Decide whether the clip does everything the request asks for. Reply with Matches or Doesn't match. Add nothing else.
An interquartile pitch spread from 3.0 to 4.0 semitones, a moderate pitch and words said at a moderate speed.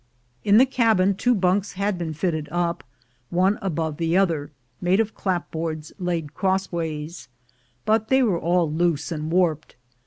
Matches